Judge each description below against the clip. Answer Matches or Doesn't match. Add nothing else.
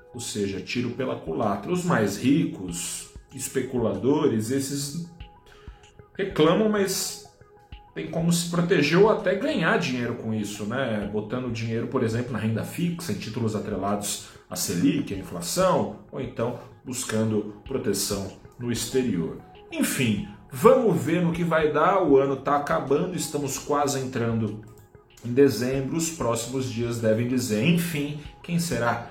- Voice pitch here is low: Matches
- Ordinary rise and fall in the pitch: Doesn't match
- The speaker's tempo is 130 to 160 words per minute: Matches